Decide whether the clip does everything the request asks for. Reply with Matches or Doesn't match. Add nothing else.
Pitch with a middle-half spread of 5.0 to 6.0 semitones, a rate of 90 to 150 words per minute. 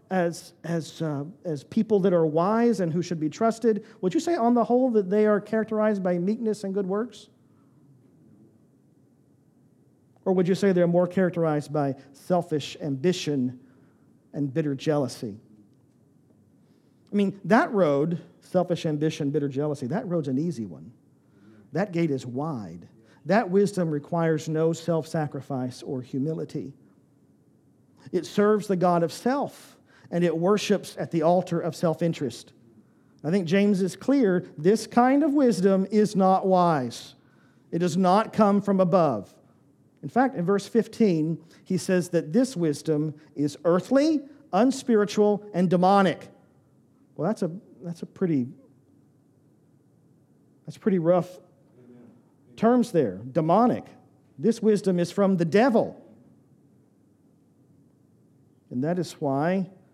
Matches